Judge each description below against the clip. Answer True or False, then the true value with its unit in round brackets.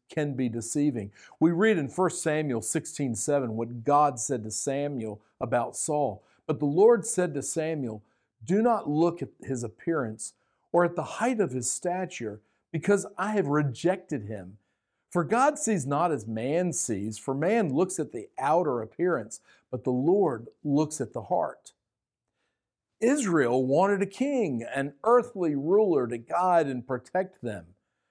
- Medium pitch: True (145 Hz)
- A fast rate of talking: False (155 wpm)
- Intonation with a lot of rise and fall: True (6.8 semitones)